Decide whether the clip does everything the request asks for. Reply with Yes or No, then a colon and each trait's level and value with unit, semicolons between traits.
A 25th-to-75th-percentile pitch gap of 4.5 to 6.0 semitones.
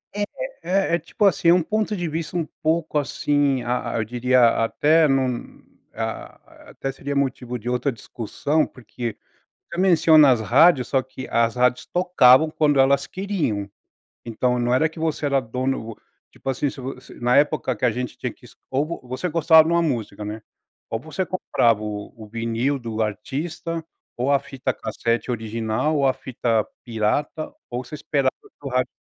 Yes: average, 4.8 semitones